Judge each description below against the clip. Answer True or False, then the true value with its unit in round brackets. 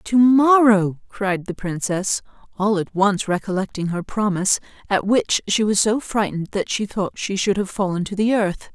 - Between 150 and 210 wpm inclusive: True (185 wpm)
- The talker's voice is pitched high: True (200 Hz)